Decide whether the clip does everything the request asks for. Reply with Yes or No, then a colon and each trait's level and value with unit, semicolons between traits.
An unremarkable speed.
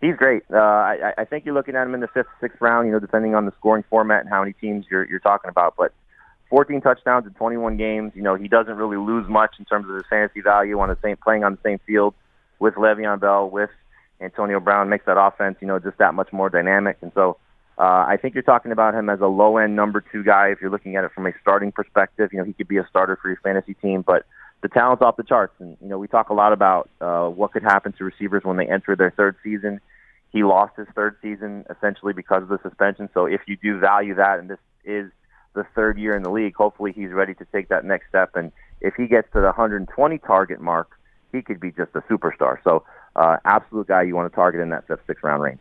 No: fast, 255 wpm